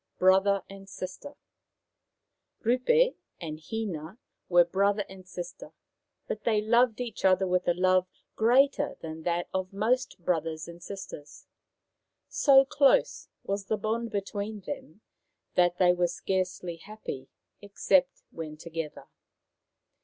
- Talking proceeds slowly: Yes, slow, 125 wpm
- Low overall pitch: No, high, 190 Hz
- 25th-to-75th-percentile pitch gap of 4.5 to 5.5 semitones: No, average, 3.8 semitones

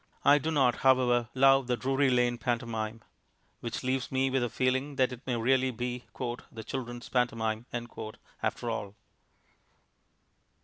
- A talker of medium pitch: No, low, 125 Hz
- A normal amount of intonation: No, narrow, 1.9 semitones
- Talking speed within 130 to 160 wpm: Yes, average, 140 wpm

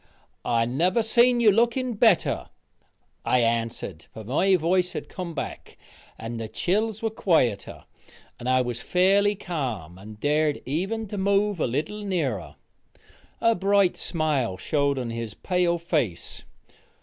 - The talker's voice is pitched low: No, medium, 165 Hz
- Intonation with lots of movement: Yes, wide, 8.6 semitones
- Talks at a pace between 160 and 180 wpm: No, average, 140 wpm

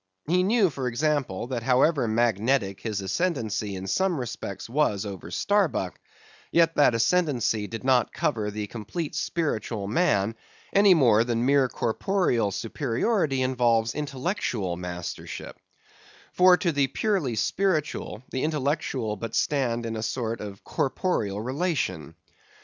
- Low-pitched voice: Yes, low, 125 Hz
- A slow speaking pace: Yes, slow, 130 wpm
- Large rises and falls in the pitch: Yes, wide, 6.1 semitones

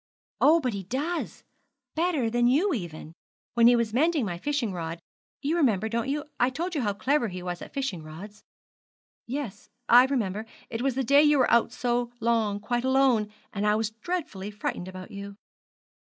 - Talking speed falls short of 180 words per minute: No, average, 185 wpm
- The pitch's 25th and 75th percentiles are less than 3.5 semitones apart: No, average, 5.1 semitones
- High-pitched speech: Yes, high, 235 Hz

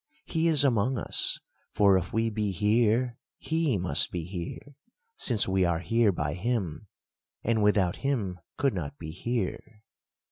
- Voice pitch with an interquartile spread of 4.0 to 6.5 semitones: Yes, average, 4.9 semitones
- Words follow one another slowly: No, average, 150 wpm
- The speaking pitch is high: No, low, 105 Hz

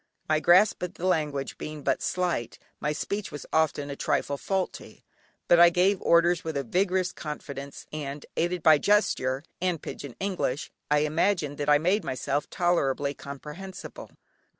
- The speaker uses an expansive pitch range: No, average, 4.1 semitones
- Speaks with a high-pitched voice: No, medium, 155 Hz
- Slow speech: No, average, 155 wpm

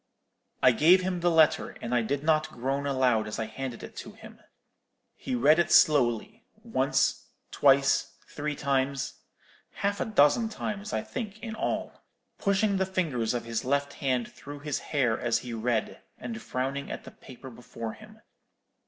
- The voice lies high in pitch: No, medium, 140 Hz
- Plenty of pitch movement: Yes, wide, 6.2 semitones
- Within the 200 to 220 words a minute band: No, average, 160 wpm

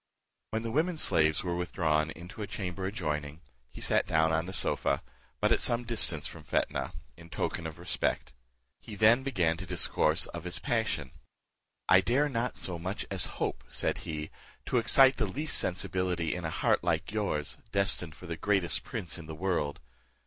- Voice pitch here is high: No, very low, 90 Hz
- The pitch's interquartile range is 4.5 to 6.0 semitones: Yes, wide, 5.4 semitones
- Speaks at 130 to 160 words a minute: No, average, 180 wpm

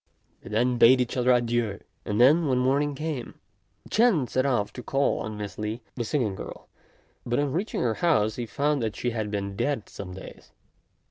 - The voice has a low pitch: Yes, low, 120 Hz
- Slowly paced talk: No, average, 190 wpm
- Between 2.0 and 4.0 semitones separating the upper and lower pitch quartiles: No, average, 4.5 semitones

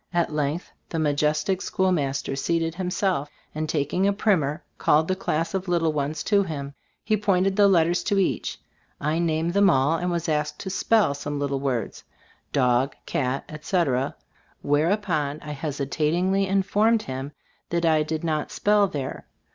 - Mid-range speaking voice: Yes, medium, 160 Hz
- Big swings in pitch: No, average, 4.4 semitones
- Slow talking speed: No, average, 160 wpm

